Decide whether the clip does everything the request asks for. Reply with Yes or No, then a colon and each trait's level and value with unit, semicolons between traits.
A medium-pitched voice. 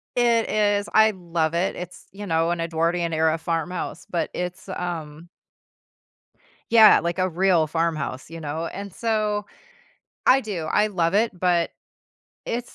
Yes: medium, 175 Hz